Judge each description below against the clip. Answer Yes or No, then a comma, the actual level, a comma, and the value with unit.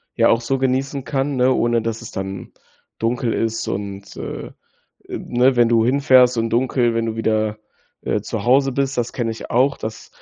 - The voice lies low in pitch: Yes, low, 120 Hz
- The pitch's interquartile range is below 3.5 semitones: Yes, narrow, 2.5 semitones